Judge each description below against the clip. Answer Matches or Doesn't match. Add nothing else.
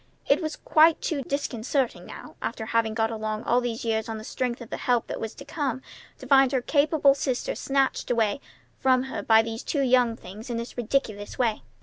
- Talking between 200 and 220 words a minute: Matches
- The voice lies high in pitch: Matches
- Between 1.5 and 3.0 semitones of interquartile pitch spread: Doesn't match